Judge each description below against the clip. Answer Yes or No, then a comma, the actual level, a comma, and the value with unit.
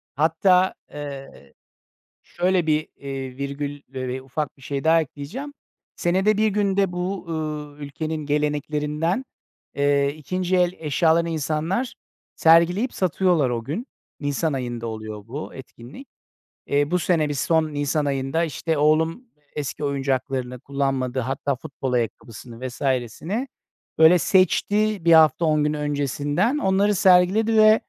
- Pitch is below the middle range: No, medium, 150 Hz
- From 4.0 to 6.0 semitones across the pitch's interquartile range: Yes, average, 4.4 semitones